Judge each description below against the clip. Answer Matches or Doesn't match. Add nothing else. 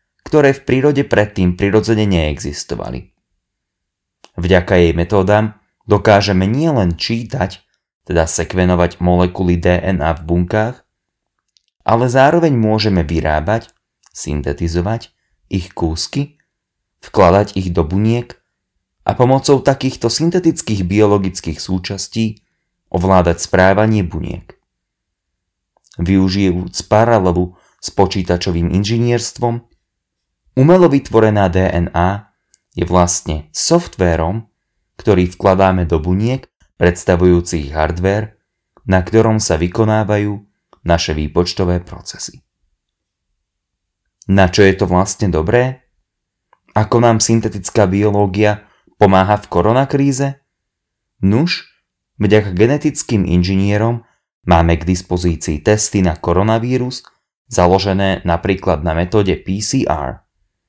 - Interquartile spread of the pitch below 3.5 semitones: Doesn't match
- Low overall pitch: Matches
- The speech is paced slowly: Matches